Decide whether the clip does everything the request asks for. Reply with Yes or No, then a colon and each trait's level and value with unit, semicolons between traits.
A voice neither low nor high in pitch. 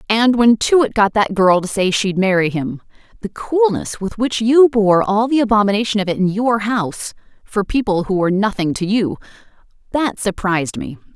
No: high, 210 Hz